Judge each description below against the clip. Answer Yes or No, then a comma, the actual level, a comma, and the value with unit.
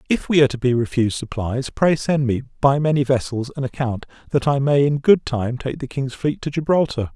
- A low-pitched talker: Yes, low, 130 Hz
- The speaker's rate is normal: No, fast, 225 wpm